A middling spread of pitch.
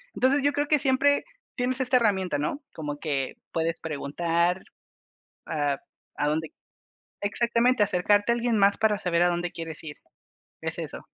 No: wide, 7.1 semitones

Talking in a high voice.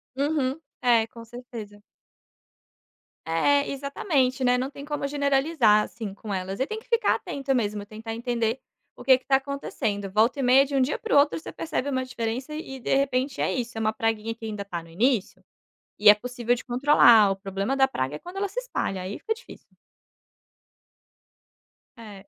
Yes: high, 245 Hz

